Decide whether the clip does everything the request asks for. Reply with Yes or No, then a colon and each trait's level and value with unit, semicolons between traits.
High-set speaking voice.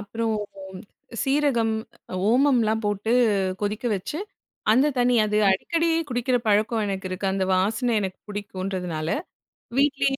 Yes: high, 220 Hz